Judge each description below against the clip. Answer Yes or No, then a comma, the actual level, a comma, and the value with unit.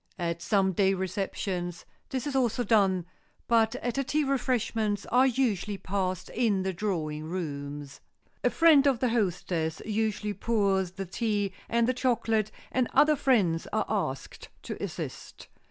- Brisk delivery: No, average, 150 wpm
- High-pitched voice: Yes, high, 205 Hz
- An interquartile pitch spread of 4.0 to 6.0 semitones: Yes, average, 4.5 semitones